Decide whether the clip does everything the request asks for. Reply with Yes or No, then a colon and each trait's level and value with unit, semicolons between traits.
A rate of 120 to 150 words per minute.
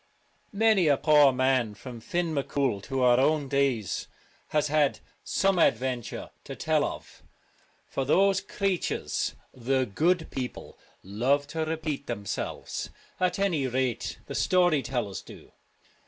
Yes: slow, 135 wpm